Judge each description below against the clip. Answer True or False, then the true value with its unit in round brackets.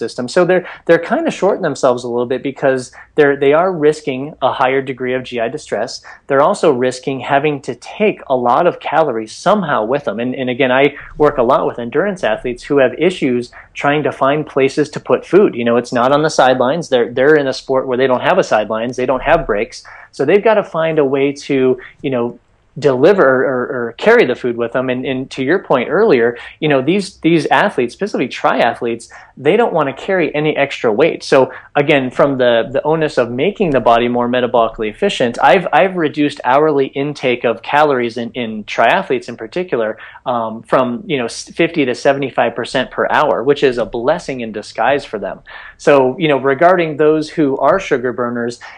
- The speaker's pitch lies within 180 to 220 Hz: False (135 Hz)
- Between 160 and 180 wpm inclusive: False (205 wpm)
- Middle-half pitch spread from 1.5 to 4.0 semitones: True (3.6 semitones)